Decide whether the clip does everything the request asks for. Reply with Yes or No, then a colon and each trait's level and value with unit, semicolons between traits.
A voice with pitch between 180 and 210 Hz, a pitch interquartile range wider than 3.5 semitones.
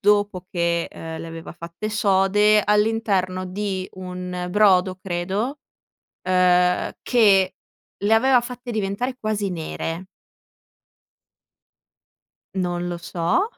No: high, 190 Hz; average, 2.9 semitones